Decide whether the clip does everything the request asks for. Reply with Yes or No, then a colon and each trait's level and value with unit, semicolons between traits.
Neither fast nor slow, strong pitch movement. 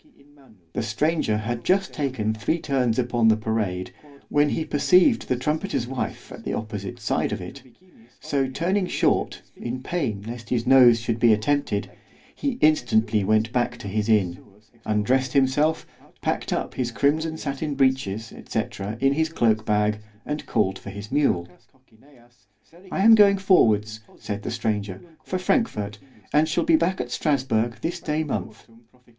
Yes: average, 150 wpm; wide, 5.7 semitones